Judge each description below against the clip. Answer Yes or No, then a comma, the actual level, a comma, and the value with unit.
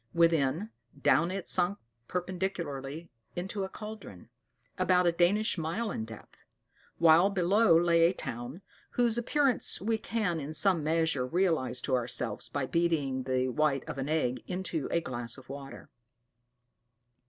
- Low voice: No, medium, 165 Hz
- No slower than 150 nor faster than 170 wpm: No, average, 140 wpm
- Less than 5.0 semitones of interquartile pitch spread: No, wide, 5.6 semitones